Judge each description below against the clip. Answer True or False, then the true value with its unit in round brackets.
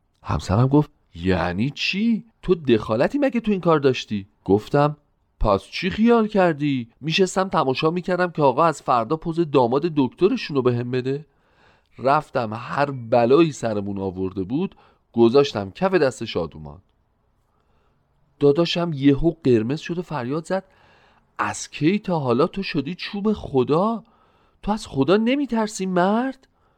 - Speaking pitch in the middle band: True (145 Hz)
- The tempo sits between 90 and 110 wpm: False (135 wpm)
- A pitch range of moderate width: False (7.8 semitones)